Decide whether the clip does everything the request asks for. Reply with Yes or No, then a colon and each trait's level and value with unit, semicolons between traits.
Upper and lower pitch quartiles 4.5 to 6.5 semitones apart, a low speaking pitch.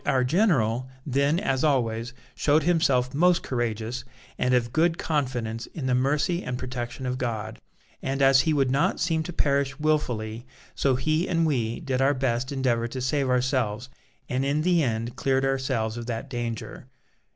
No: average, 3.3 semitones; low, 130 Hz